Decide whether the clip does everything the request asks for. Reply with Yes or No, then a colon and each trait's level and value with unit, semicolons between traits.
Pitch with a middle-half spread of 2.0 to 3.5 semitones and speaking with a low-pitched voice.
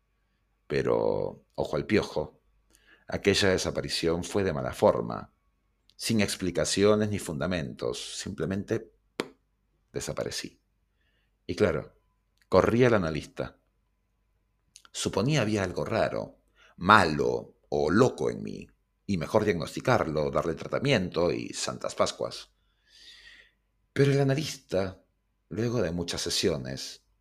No: average, 4.8 semitones; low, 100 Hz